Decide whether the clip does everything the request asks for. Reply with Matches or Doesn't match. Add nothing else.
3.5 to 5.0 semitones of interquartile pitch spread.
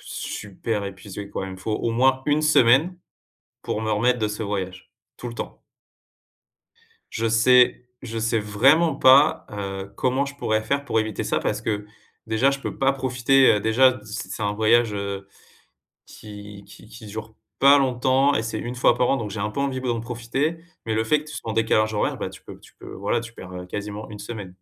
Matches